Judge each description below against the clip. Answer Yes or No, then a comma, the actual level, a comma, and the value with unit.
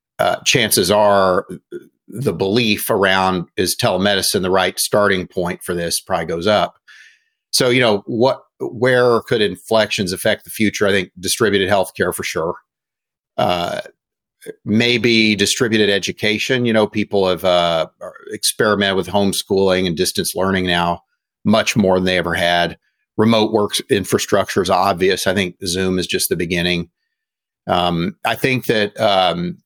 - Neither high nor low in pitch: No, low, 100 Hz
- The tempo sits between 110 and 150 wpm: Yes, average, 145 wpm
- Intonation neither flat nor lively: Yes, average, 3.6 semitones